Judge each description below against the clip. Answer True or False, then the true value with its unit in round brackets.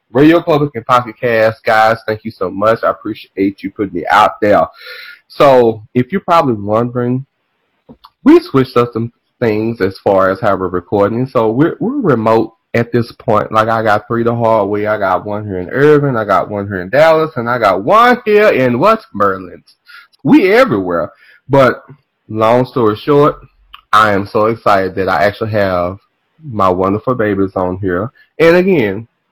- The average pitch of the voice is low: True (115 Hz)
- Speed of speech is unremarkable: True (180 wpm)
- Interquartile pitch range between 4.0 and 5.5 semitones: True (5.1 semitones)